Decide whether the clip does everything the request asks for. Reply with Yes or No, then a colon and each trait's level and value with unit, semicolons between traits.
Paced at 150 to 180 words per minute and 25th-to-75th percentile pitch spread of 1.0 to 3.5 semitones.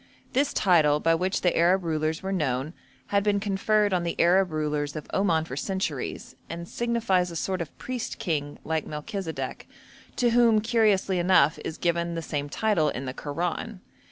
No: average, 175 wpm; average, 4.3 semitones